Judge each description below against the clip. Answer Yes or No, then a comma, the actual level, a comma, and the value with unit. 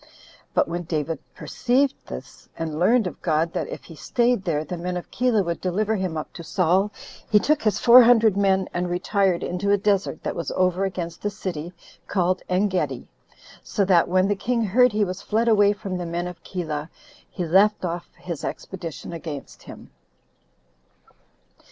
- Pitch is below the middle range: No, medium, 185 Hz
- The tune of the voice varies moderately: Yes, average, 3.3 semitones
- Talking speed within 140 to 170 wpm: No, average, 180 wpm